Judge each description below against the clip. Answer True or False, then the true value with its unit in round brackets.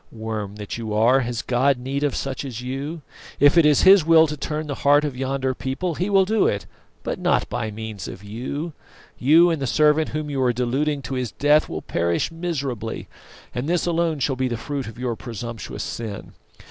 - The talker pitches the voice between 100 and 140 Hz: True (135 Hz)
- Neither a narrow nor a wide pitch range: True (4.3 semitones)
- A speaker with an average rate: False (210 wpm)